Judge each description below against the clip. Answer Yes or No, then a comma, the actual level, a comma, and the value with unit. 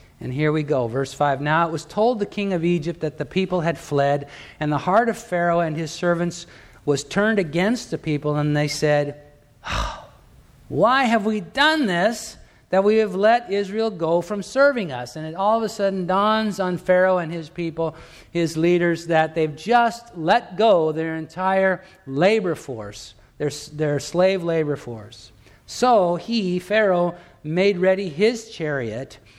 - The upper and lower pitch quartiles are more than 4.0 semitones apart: Yes, average, 5.2 semitones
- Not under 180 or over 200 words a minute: No, average, 170 wpm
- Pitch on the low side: No, medium, 170 Hz